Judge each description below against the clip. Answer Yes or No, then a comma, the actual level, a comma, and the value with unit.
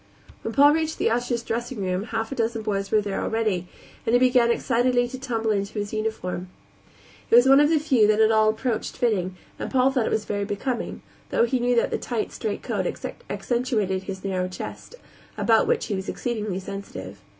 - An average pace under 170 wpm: No, average, 200 wpm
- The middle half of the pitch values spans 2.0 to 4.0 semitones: Yes, average, 3.4 semitones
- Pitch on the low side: No, high, 225 Hz